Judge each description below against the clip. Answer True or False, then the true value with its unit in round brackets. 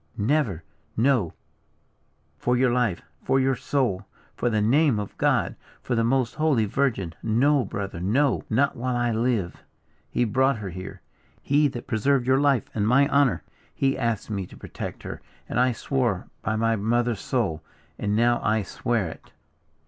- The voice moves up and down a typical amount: True (3.9 semitones)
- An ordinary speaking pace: True (165 wpm)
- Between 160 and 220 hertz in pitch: False (120 Hz)